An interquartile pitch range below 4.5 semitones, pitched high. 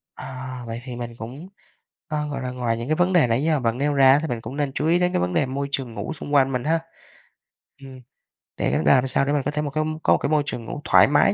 No: average, 3.1 semitones; low, 135 Hz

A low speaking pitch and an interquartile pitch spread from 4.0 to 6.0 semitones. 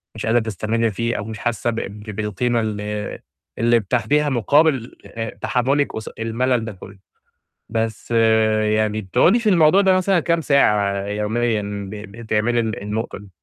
No: low, 115 Hz; average, 2.9 semitones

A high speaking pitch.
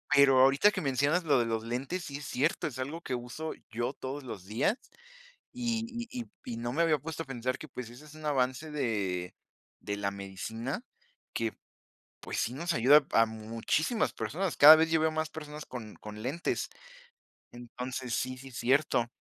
No: low, 130 Hz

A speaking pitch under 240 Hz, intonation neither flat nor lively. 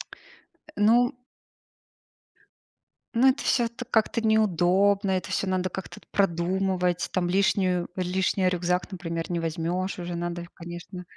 No: medium, 185 Hz; narrow, 2.1 semitones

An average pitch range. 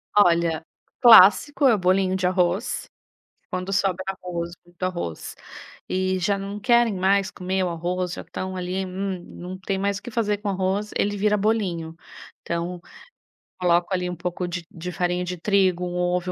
No: narrow, 1.9 semitones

